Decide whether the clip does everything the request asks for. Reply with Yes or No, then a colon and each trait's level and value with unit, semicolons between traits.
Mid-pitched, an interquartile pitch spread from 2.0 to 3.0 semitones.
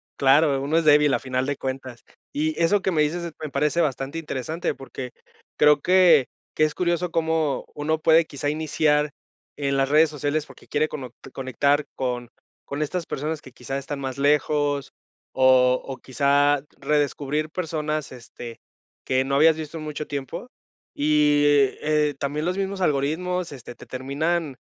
Yes: medium, 150 Hz; narrow, 2.5 semitones